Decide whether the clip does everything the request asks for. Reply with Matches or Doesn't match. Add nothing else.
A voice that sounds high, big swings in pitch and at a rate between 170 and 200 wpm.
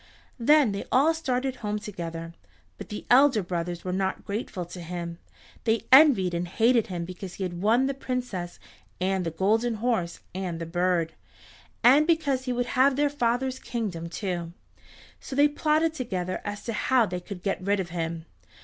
Matches